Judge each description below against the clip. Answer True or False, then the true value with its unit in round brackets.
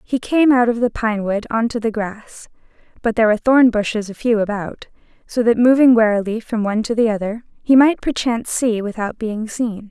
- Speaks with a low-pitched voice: False (225 Hz)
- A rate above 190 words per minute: True (200 wpm)